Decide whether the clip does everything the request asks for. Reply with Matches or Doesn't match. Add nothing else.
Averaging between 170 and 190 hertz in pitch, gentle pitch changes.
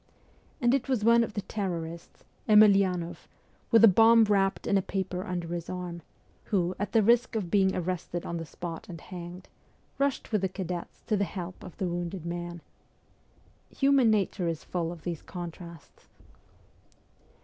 Doesn't match